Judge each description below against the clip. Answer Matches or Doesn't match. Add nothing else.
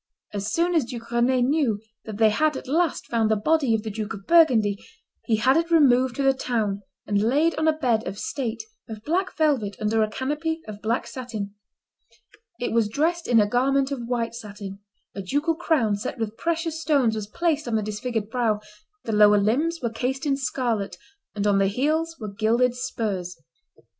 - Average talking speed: Matches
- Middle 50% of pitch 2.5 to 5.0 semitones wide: Doesn't match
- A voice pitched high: Matches